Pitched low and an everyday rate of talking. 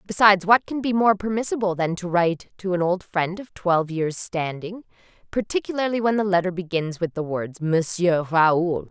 No: medium, 185 Hz; average, 180 wpm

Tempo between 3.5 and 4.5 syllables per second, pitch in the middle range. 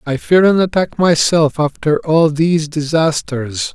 Yes: 4.1 syllables/s; medium, 155 Hz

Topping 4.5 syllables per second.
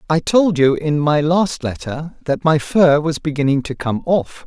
No: 4.3 syllables/s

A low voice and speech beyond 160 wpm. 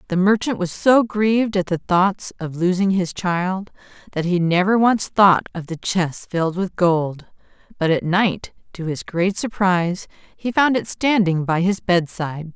No: medium, 185 Hz; average, 175 wpm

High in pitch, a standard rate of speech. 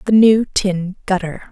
Yes: high, 195 Hz; average, 160 wpm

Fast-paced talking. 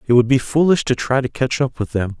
Yes: fast, 300 wpm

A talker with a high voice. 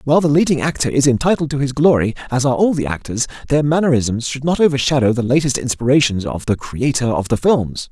No: low, 135 Hz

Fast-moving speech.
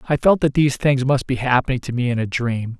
Yes: fast, 280 wpm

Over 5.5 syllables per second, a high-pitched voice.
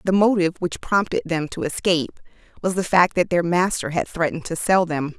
No: 5.7 syllables/s; medium, 170 Hz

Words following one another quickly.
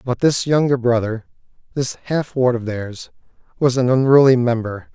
No: average, 160 wpm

